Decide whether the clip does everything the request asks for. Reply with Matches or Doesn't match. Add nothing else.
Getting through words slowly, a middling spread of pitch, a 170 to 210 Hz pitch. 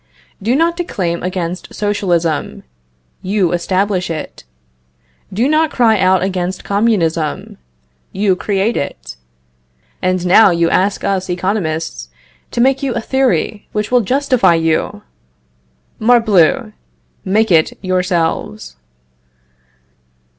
Matches